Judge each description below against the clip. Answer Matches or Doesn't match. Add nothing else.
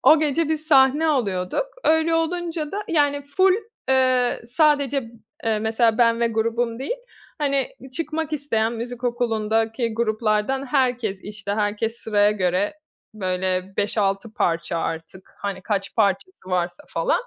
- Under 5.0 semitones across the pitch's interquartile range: Doesn't match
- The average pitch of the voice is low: Doesn't match